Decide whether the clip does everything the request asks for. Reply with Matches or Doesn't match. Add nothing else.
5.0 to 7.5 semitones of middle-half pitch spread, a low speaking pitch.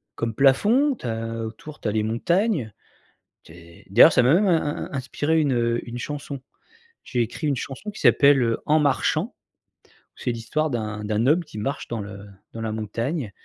Matches